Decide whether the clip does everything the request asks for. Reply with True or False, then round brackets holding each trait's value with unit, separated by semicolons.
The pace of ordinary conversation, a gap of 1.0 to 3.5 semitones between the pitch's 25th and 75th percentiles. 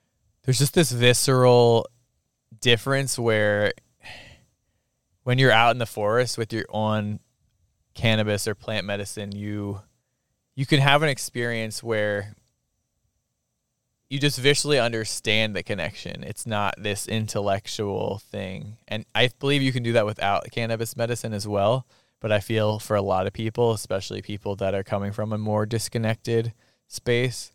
True (145 wpm; 2.8 semitones)